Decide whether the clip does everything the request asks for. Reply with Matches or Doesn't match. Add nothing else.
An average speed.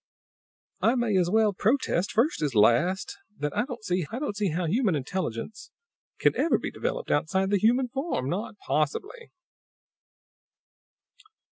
Doesn't match